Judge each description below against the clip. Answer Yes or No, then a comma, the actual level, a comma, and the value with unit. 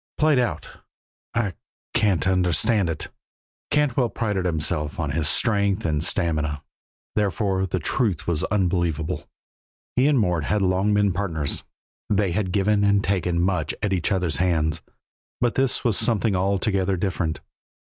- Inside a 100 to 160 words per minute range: Yes, average, 140 wpm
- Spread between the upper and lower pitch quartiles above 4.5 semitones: No, average, 3.7 semitones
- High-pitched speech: No, very low, 95 Hz